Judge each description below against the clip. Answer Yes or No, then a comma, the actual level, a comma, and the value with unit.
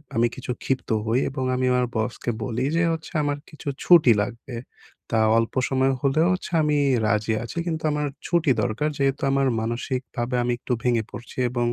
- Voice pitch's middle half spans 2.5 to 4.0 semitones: Yes, average, 3.5 semitones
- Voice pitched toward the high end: No, low, 130 Hz